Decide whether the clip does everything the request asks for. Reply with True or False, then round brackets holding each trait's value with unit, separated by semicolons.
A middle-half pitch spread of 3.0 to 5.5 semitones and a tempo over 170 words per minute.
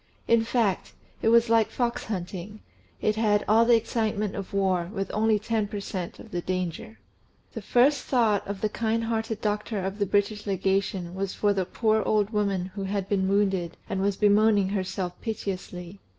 False (2.4 semitones; 180 wpm)